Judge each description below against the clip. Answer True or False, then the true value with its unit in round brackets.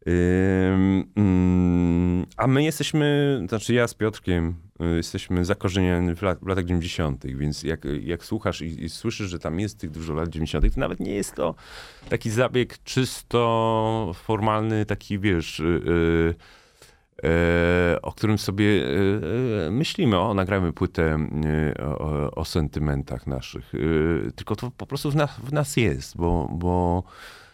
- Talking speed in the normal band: True (145 wpm)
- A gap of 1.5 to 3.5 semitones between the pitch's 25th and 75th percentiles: False (4.7 semitones)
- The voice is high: False (90 Hz)